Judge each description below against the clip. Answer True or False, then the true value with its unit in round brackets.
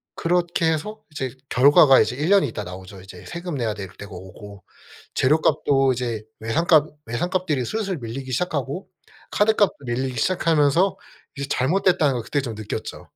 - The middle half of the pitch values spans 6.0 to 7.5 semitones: True (6.8 semitones)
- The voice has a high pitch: False (140 Hz)